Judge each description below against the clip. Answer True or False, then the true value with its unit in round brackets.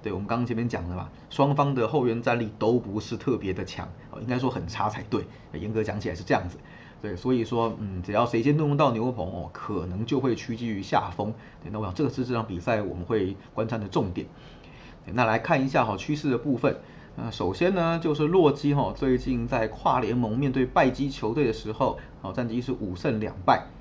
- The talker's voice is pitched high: False (120 Hz)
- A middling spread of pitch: True (3.9 semitones)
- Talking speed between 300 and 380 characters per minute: True (320 characters per minute)